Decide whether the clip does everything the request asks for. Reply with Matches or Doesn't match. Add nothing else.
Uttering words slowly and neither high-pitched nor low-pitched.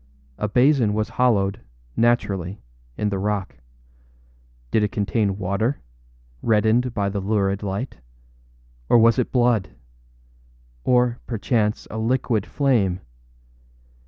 Doesn't match